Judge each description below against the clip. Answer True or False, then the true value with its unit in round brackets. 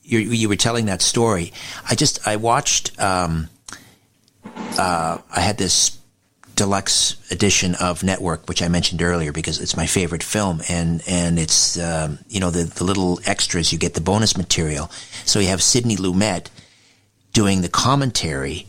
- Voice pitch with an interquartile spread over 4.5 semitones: False (3.7 semitones)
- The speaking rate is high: False (165 wpm)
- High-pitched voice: False (95 Hz)